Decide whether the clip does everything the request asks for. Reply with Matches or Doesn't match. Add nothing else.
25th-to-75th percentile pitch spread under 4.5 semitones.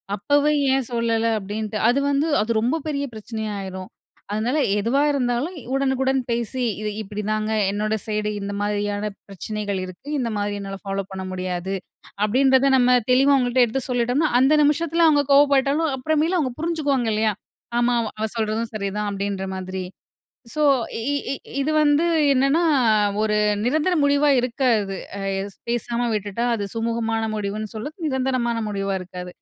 Doesn't match